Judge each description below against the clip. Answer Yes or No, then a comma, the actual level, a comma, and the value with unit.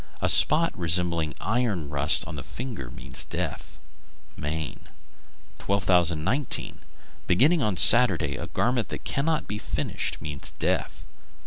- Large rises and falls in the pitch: Yes, wide, 8.1 semitones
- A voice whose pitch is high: No, very low, 90 Hz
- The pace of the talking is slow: Yes, slow, 120 wpm